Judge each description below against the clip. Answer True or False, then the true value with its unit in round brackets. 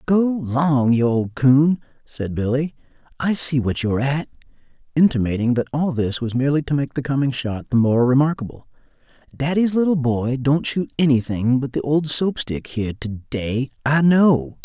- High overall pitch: False (135 Hz)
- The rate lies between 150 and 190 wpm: True (170 wpm)